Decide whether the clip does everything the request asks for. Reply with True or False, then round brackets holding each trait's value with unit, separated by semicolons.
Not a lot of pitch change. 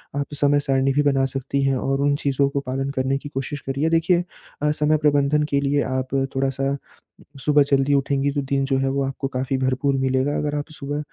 True (1.2 semitones)